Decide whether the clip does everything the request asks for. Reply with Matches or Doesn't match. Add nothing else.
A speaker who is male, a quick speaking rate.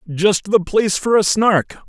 Doesn't match